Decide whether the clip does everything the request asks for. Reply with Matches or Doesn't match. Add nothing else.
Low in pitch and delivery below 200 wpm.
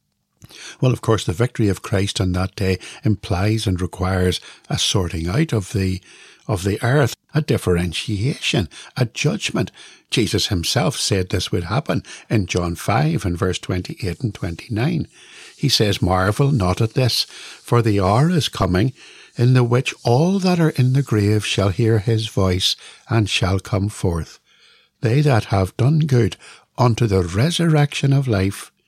Matches